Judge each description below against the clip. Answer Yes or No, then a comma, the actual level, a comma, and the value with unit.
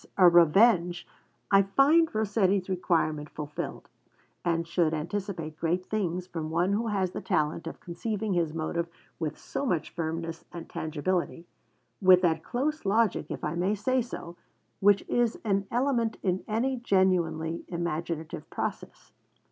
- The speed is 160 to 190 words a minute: No, average, 140 wpm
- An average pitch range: Yes, average, 4.0 semitones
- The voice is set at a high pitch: No, medium, 180 Hz